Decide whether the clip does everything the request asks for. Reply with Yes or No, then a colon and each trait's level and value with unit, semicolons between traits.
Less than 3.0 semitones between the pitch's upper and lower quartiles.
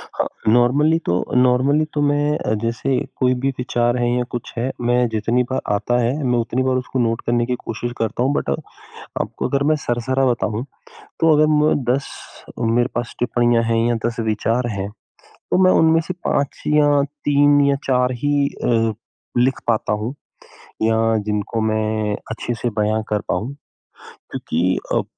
No: average, 3.3 semitones